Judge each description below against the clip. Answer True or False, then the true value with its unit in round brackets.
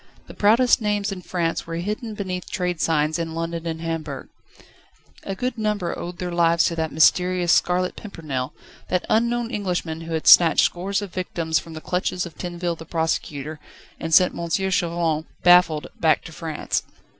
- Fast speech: False (170 wpm)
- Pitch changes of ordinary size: False (2.3 semitones)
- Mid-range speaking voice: True (175 Hz)